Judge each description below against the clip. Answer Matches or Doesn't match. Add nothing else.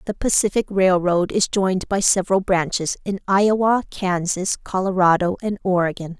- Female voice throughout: Matches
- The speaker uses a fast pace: Doesn't match